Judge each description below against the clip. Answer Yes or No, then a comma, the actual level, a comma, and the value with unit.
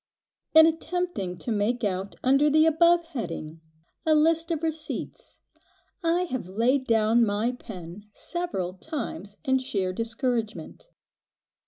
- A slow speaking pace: Yes, slow, 125 wpm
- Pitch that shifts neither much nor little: No, wide, 7.7 semitones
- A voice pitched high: Yes, very high, 250 Hz